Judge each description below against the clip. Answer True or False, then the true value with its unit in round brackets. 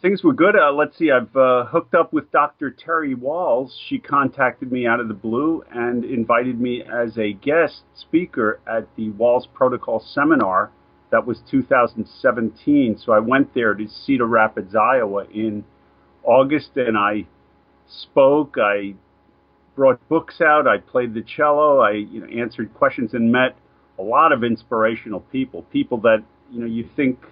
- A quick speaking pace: False (165 wpm)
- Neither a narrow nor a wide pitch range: True (4.7 semitones)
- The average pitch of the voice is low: True (120 Hz)